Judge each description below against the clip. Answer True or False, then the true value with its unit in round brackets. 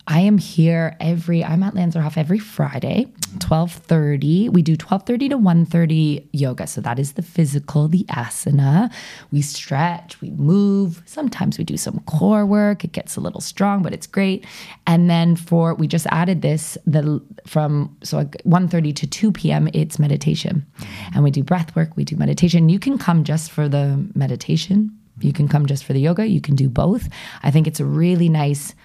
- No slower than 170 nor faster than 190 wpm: True (185 wpm)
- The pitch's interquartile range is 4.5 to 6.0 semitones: False (3.5 semitones)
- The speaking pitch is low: False (165 Hz)